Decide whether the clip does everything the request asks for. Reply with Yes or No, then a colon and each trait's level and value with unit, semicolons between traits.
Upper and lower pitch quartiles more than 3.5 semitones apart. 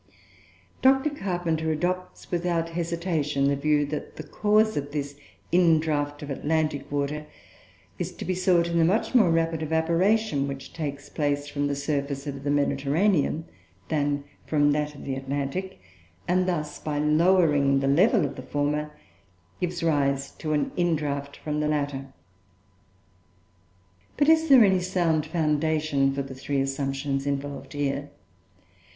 No: average, 3.1 semitones